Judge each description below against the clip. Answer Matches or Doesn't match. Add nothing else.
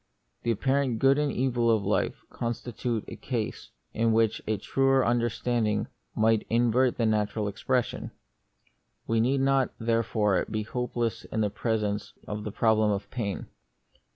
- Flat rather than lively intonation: Matches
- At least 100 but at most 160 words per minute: Matches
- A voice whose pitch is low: Matches